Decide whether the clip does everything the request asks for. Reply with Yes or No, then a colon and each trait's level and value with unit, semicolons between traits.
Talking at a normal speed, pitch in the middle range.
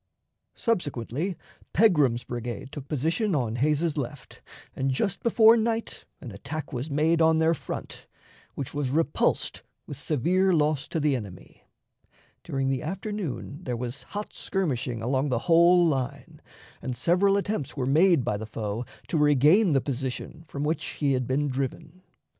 Yes: average, 155 wpm; medium, 145 Hz